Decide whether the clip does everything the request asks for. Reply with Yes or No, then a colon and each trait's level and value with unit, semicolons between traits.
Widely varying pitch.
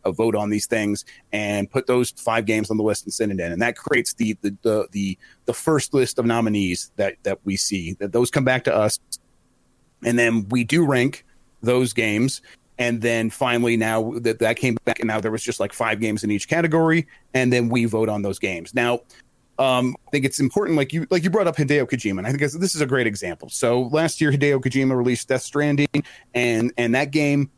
No: average, 3.8 semitones